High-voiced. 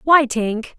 Yes: very high, 250 Hz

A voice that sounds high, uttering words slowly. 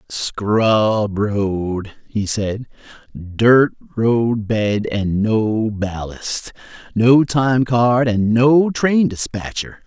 No: low, 110 Hz; slow, 105 wpm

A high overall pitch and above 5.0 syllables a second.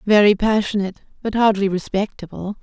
Yes: high, 205 Hz; 5.9 syllables/s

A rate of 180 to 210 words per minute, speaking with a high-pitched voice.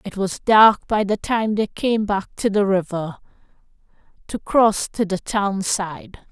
No: average, 170 wpm; high, 200 Hz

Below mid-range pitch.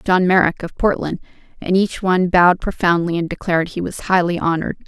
No: medium, 180 Hz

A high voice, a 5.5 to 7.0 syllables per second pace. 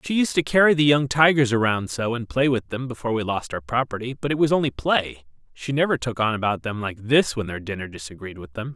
No: low, 125 Hz; 6.0 syllables/s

